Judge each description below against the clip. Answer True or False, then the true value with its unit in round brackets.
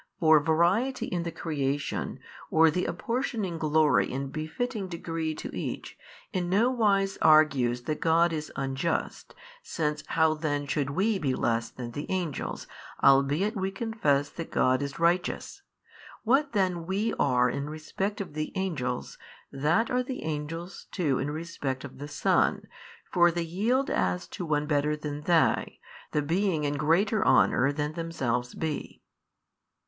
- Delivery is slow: False (150 wpm)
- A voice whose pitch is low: False (160 Hz)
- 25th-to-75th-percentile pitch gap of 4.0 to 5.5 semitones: True (4.4 semitones)